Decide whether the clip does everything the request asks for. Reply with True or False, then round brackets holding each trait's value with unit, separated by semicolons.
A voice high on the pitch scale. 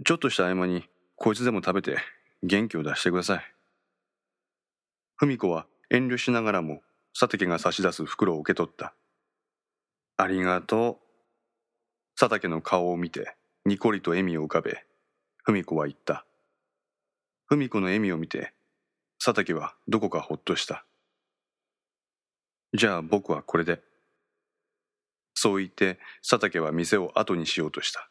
False (95 Hz)